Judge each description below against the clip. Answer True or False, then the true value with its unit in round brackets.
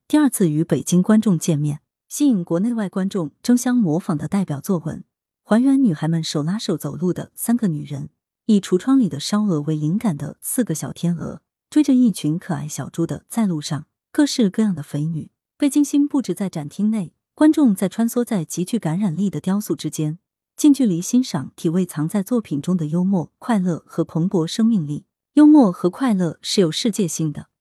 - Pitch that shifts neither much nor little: False (6.2 semitones)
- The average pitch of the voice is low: False (185 Hz)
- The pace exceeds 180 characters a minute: True (295 characters per minute)